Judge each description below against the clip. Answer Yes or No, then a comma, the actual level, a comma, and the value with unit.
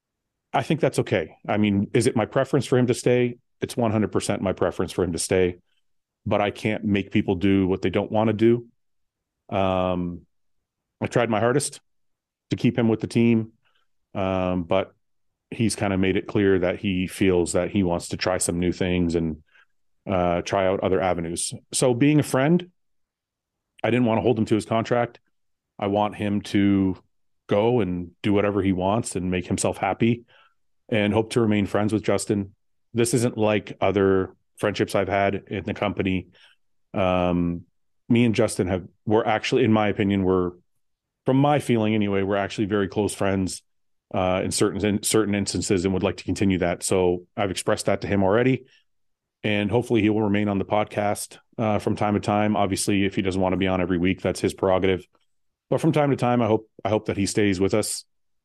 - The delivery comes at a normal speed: Yes, average, 195 wpm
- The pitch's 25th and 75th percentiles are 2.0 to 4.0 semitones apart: Yes, average, 2.9 semitones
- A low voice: Yes, low, 100 Hz